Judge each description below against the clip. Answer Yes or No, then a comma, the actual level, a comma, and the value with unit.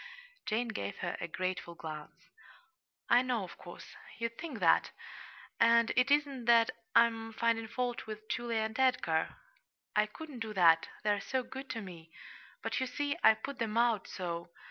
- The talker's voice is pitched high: Yes, high, 225 Hz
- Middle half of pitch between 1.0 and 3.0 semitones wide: No, average, 4.7 semitones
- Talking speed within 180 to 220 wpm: No, average, 165 wpm